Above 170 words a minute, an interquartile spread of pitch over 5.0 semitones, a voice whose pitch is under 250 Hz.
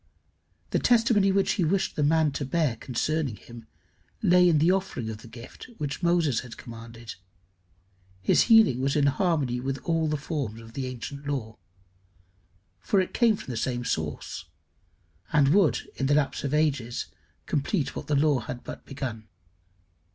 No: average, 165 wpm; wide, 5.4 semitones; medium, 140 Hz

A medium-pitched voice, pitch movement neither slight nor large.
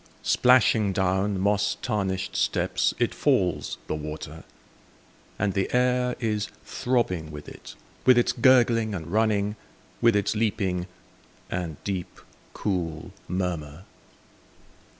No: low, 100 Hz; average, 3.9 semitones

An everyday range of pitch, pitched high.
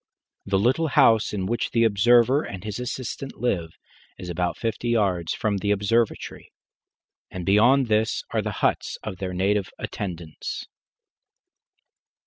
No: average, 3.9 semitones; low, 105 Hz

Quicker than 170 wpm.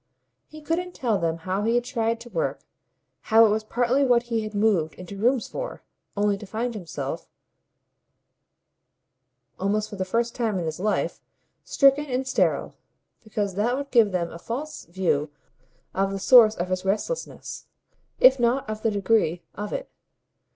No: average, 165 wpm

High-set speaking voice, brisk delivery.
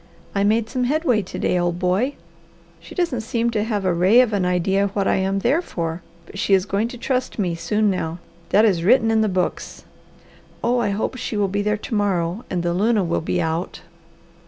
Yes: high, 205 Hz; fast, 220 wpm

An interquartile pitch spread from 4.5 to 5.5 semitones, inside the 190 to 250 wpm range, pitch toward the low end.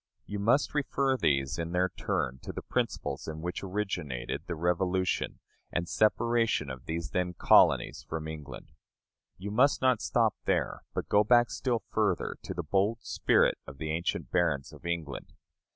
No: average, 5.2 semitones; average, 165 wpm; very low, 90 Hz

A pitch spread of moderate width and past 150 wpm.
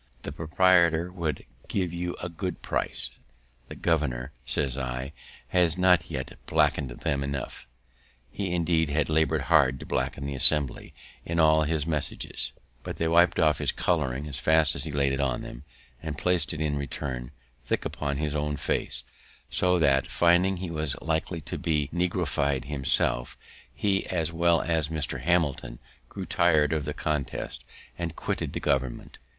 Yes: average, 3.4 semitones; average, 160 wpm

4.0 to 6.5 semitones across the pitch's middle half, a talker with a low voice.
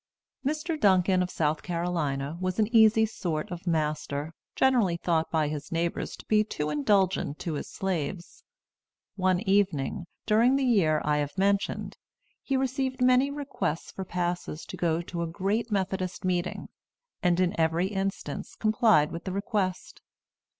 No: average, 4.6 semitones; medium, 185 Hz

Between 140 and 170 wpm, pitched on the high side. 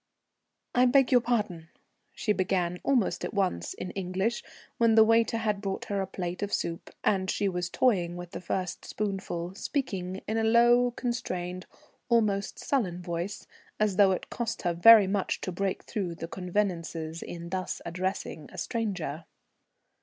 Yes: average, 160 wpm; high, 195 Hz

